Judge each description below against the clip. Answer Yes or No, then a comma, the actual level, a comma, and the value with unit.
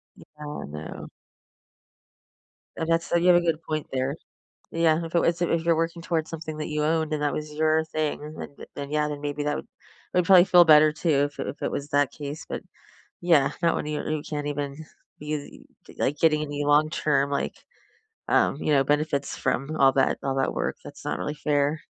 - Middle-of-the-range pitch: Yes, medium, 150 Hz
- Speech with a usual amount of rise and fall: No, narrow, 1.9 semitones